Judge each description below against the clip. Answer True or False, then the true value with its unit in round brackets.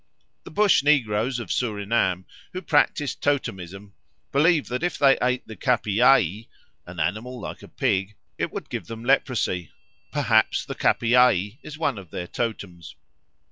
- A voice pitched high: False (115 Hz)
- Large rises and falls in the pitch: True (5.7 semitones)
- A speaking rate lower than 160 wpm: True (145 wpm)